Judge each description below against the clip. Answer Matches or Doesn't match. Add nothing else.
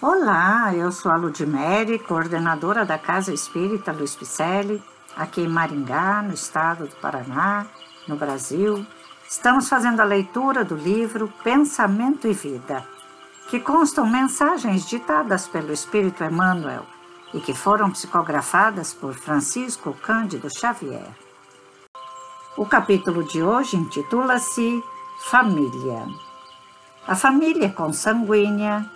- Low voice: Doesn't match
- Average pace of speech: Doesn't match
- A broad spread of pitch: Matches